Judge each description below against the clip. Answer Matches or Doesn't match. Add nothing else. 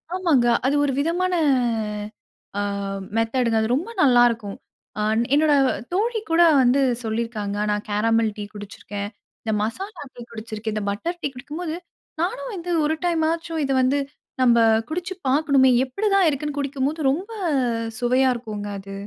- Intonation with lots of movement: Matches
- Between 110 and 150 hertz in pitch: Doesn't match